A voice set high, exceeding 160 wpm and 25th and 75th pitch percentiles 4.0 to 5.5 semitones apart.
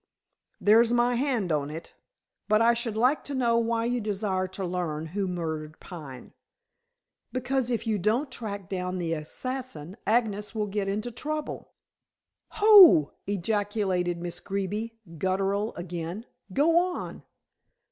No: high, 205 Hz; slow, 135 wpm; average, 4.8 semitones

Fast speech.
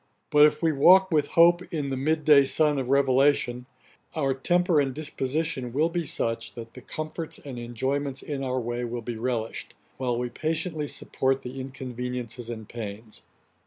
No: average, 170 wpm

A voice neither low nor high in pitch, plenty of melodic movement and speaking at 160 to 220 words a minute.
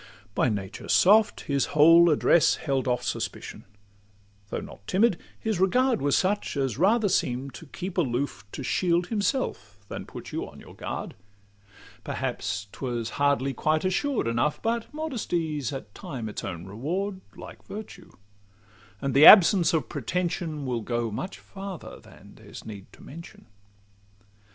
No: medium, 155 Hz; wide, 7.3 semitones; average, 150 wpm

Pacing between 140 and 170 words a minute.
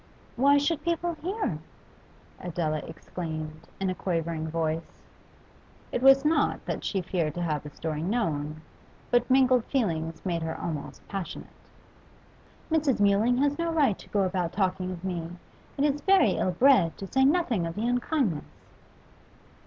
Yes: average, 155 wpm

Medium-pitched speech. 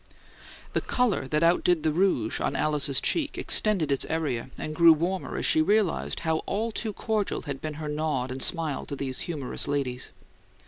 Yes: medium, 155 Hz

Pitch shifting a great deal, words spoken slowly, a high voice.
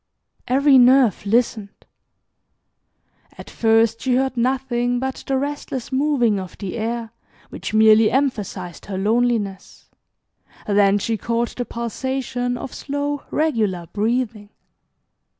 No: average, 3.6 semitones; slow, 115 wpm; high, 235 Hz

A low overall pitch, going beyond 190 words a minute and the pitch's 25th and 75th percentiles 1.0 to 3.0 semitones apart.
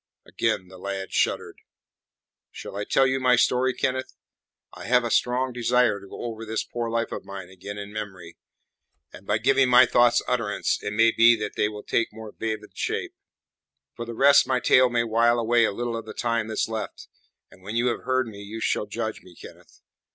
Yes: low, 115 Hz; fast, 205 wpm; average, 2.7 semitones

